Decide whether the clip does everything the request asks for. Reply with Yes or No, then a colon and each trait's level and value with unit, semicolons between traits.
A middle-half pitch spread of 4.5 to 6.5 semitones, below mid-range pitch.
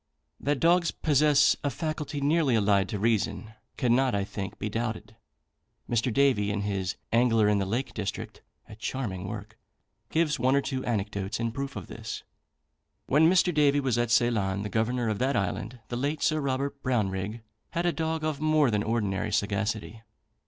Yes: average, 5.2 semitones; low, 120 Hz